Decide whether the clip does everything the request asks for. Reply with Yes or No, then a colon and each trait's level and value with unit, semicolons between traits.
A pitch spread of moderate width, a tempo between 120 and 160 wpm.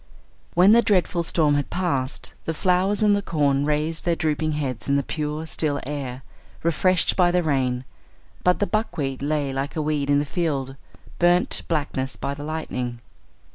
No: average, 3.9 semitones; average, 175 wpm